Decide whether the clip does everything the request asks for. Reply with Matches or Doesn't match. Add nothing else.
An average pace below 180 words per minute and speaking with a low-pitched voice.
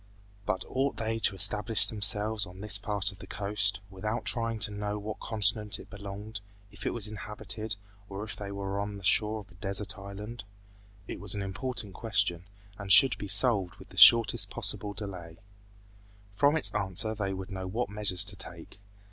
Doesn't match